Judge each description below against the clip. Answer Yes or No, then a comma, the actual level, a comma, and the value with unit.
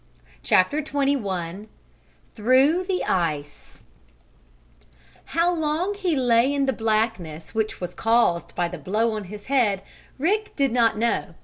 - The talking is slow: Yes, slow, 130 wpm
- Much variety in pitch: Yes, wide, 6.9 semitones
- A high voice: Yes, high, 230 Hz